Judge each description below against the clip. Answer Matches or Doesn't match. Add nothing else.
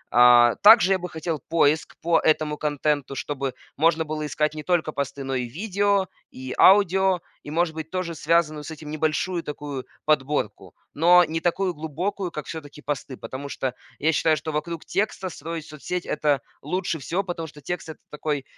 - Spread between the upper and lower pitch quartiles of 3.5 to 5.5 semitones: Doesn't match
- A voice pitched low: Doesn't match